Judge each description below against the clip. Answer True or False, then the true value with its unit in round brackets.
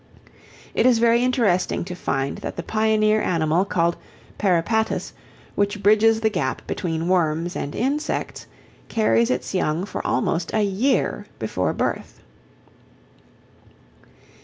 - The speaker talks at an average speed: False (120 wpm)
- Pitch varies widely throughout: False (4.8 semitones)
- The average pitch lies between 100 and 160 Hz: False (195 Hz)